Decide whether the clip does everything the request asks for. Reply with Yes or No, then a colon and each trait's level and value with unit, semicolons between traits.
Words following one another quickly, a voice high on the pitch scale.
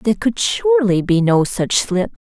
No: average, 185 wpm; high, 215 Hz